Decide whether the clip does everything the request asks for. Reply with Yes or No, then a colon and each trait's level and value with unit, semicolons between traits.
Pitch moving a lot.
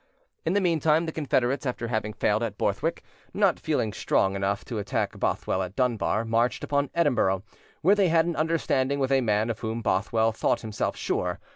Yes: wide, 6.5 semitones